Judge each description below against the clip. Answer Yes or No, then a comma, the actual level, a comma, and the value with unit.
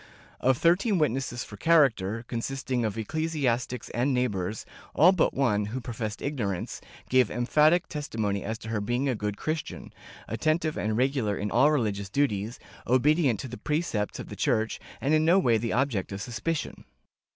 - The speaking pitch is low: Yes, low, 125 Hz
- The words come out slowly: No, average, 175 wpm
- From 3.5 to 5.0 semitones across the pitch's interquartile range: No, wide, 5.4 semitones